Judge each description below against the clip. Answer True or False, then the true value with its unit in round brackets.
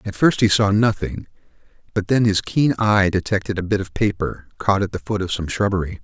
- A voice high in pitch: False (100 Hz)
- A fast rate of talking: True (220 wpm)